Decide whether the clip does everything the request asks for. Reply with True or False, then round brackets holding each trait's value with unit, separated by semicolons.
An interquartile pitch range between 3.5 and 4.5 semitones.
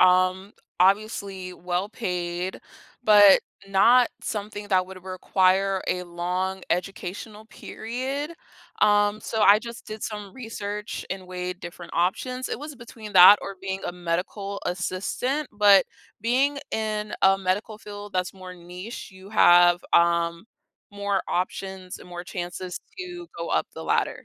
False (2.7 semitones)